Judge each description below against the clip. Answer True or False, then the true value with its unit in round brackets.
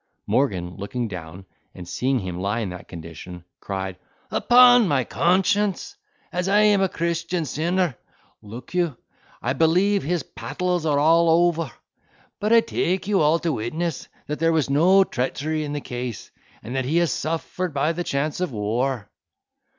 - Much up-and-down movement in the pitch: True (6.7 semitones)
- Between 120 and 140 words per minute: False (165 wpm)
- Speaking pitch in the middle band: True (155 Hz)